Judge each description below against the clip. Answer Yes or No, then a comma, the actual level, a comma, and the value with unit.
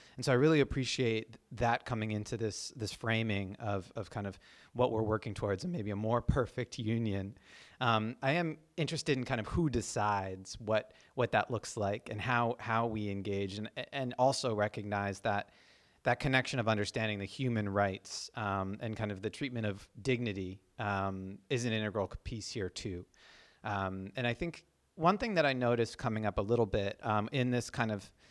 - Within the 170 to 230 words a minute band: Yes, average, 190 wpm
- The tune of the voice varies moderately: Yes, average, 3.3 semitones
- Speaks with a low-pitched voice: Yes, low, 110 Hz